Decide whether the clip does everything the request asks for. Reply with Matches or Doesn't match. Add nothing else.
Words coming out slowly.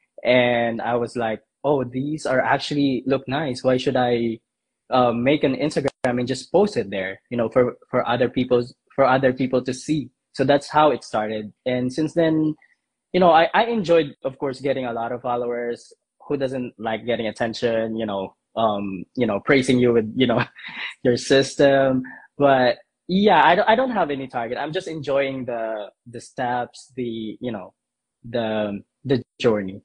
Doesn't match